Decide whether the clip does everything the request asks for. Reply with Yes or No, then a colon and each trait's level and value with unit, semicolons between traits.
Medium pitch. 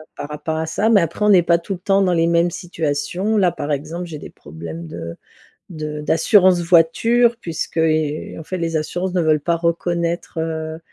Yes: medium, 165 Hz